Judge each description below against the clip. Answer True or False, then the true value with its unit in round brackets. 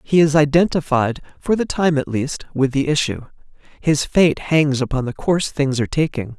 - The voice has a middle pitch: True (145 Hz)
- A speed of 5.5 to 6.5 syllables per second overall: False (5.1 syllables/s)